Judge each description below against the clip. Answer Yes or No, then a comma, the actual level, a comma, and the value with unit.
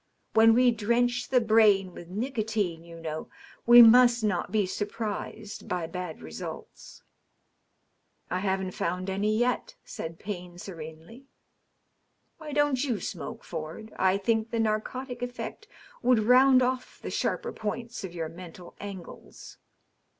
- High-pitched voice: Yes, high, 215 Hz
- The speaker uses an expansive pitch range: No, average, 5.0 semitones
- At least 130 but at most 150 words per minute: Yes, average, 140 wpm